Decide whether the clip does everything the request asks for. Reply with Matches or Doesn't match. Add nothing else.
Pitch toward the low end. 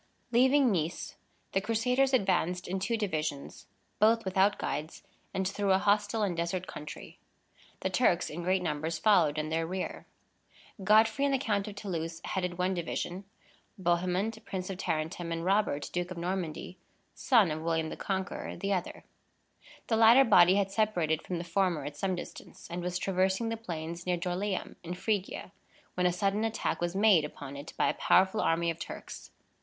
Doesn't match